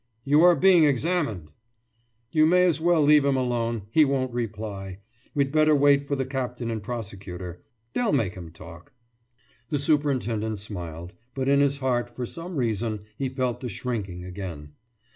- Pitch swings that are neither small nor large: No, wide, 5.9 semitones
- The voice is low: Yes, low, 125 Hz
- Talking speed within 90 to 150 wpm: No, average, 160 wpm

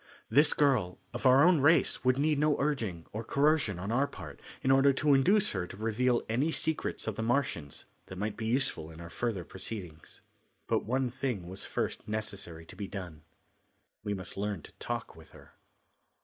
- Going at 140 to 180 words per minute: No, average, 190 wpm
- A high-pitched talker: No, low, 115 Hz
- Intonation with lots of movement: Yes, wide, 6.6 semitones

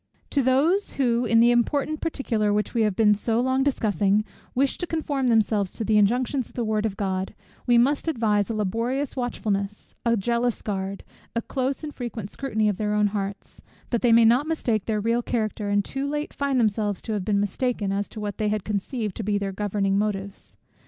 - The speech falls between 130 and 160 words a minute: No, fast, 205 wpm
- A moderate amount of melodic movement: Yes, average, 3.5 semitones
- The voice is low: No, high, 220 Hz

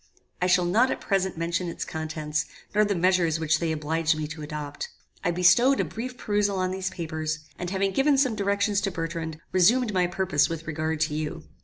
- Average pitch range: Yes, average, 3.8 semitones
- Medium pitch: Yes, medium, 175 Hz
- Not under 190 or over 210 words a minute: Yes, average, 200 wpm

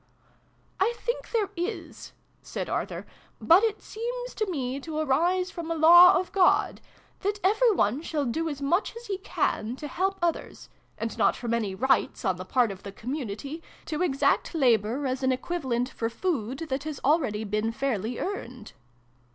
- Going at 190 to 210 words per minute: No, average, 175 wpm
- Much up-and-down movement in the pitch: Yes, wide, 7.1 semitones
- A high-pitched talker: Yes, very high, 295 Hz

